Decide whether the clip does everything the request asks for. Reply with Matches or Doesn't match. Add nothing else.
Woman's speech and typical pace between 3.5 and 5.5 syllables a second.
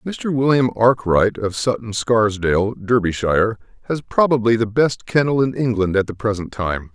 Doesn't match